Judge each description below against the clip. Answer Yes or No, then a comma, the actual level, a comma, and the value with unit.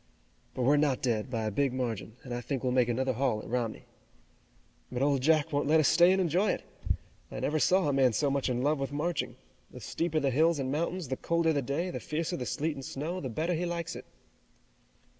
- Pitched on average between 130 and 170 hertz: Yes, medium, 140 Hz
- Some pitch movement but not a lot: Yes, average, 4.2 semitones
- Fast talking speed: Yes, fast, 235 wpm